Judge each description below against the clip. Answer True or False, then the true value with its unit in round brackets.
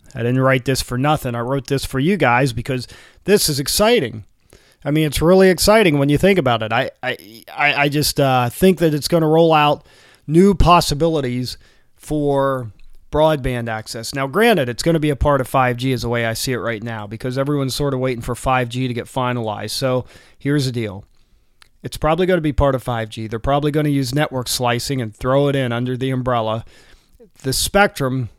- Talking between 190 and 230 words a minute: True (200 wpm)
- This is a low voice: True (130 Hz)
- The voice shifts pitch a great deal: False (3.8 semitones)